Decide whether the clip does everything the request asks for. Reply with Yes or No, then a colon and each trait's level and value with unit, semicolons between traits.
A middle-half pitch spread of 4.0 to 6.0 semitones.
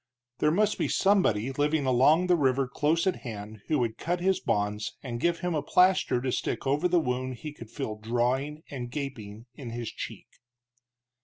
Yes: average, 5.2 semitones